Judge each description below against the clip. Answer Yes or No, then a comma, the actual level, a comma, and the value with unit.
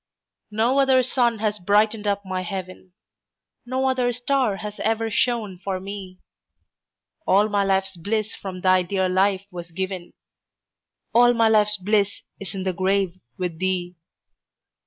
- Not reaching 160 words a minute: Yes, average, 145 wpm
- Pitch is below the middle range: No, high, 200 Hz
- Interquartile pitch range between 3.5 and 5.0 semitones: No, average, 3.0 semitones